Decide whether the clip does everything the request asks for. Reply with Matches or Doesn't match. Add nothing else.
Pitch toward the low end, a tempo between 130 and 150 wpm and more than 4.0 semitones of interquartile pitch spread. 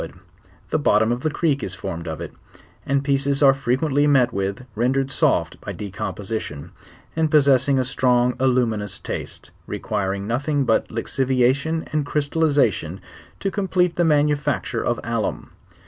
Matches